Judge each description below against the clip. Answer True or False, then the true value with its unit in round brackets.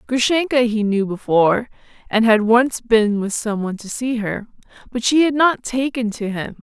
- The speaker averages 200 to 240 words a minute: False (190 wpm)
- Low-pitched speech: False (230 Hz)